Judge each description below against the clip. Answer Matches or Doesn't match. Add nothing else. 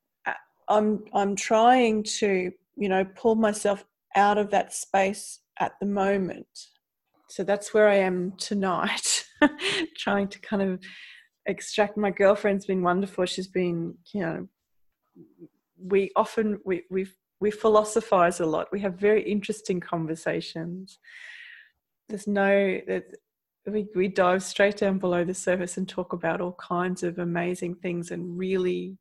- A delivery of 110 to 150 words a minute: Matches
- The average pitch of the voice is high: Matches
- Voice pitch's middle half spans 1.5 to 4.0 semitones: Matches